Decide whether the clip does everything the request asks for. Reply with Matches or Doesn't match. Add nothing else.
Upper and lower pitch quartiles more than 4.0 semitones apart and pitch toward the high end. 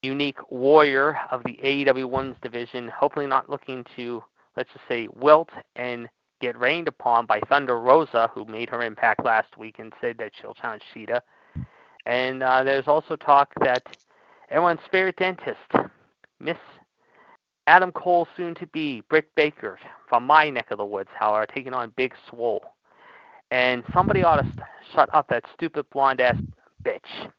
Doesn't match